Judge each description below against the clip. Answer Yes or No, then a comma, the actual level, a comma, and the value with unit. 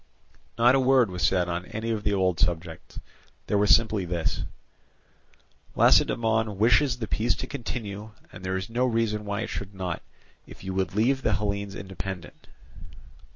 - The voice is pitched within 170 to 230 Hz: No, low, 105 Hz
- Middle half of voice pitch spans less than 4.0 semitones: Yes, average, 3.4 semitones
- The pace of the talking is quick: No, average, 165 wpm